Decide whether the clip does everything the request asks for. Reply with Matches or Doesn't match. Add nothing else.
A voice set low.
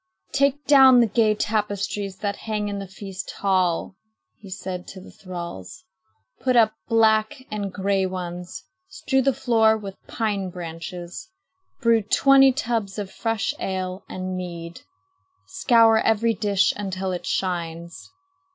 Doesn't match